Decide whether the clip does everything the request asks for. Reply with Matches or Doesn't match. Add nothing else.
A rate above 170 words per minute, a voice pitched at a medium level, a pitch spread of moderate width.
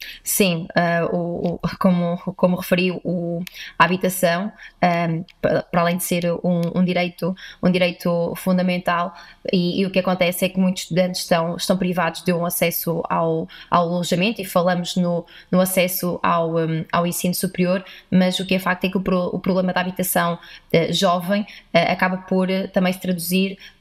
Doesn't match